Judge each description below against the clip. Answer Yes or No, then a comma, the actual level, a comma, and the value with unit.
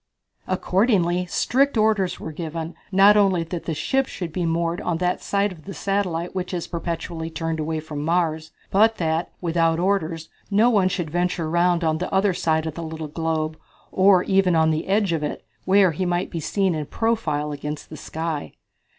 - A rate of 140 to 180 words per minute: No, average, 190 wpm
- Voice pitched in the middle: Yes, medium, 170 Hz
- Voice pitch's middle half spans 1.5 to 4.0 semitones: Yes, average, 3.0 semitones